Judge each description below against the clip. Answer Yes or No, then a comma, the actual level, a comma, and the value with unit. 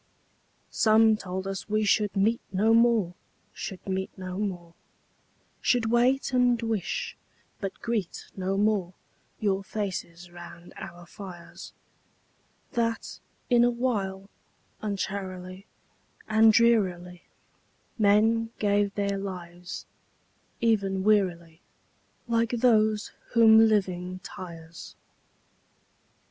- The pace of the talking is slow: Yes, slow, 100 wpm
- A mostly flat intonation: No, average, 3.4 semitones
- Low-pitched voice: No, high, 200 Hz